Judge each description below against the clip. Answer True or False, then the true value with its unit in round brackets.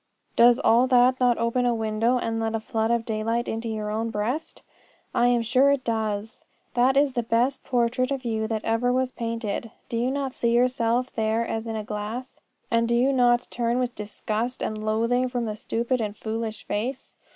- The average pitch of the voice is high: True (235 Hz)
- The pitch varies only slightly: True (2.1 semitones)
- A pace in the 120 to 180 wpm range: False (200 wpm)